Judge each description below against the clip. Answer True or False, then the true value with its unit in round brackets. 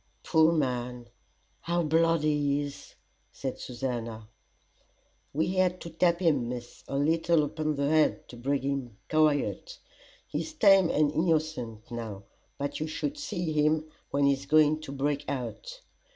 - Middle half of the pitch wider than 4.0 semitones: False (3.5 semitones)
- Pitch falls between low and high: True (150 Hz)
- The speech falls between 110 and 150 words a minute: True (145 wpm)